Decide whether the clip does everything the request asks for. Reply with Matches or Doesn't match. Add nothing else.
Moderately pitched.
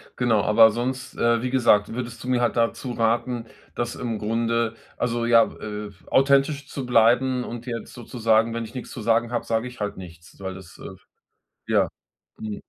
Doesn't match